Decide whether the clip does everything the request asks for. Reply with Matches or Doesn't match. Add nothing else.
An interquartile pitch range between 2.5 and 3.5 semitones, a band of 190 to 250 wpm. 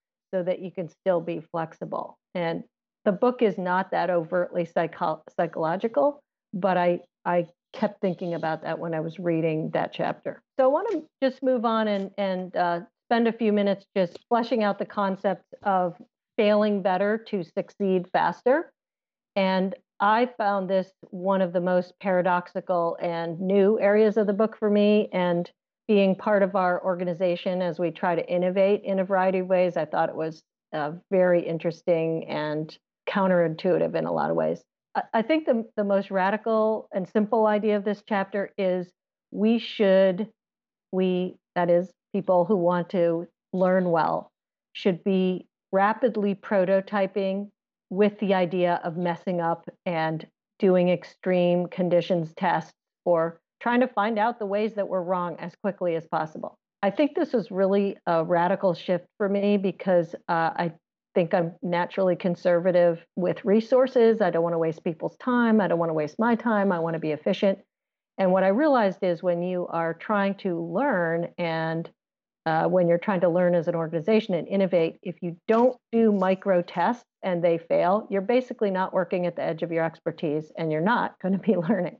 Doesn't match